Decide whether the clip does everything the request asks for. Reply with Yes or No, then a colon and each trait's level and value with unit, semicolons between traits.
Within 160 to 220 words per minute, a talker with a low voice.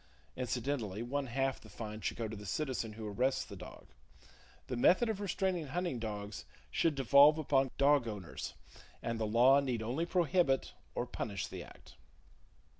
Yes: average, 165 wpm; low, 130 Hz